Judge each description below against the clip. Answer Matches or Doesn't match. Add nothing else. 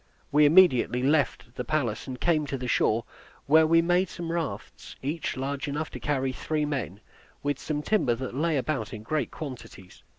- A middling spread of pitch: Matches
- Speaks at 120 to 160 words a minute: Doesn't match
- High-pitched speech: Doesn't match